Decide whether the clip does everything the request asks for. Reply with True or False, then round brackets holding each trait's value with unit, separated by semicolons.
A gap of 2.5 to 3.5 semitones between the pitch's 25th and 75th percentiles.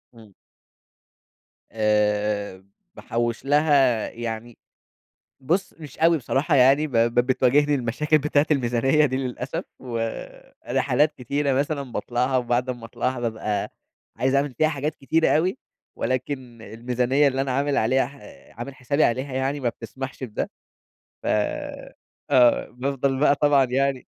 True (3.1 semitones)